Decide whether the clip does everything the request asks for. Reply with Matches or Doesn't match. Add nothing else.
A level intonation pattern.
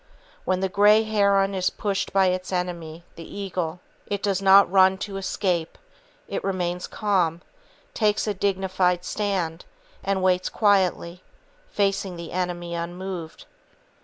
Matches